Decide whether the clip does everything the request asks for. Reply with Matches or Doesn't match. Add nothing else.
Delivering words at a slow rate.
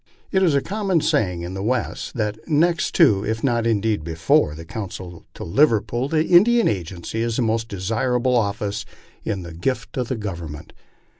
Doesn't match